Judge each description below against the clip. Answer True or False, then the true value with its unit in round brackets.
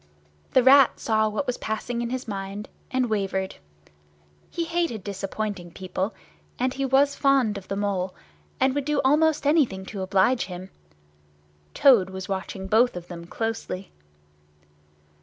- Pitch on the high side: True (215 Hz)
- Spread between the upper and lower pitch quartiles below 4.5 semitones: False (5.4 semitones)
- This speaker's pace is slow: False (145 wpm)